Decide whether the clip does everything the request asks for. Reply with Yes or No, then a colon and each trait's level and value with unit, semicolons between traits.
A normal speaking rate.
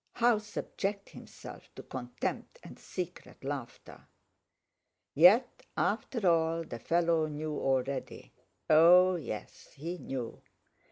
No: slow, 100 wpm